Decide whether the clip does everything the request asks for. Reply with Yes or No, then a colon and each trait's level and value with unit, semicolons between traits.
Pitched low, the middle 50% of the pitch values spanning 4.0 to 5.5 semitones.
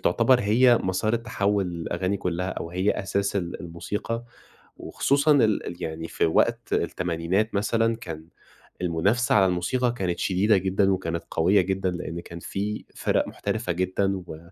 No: very low, 95 Hz; average, 3.5 semitones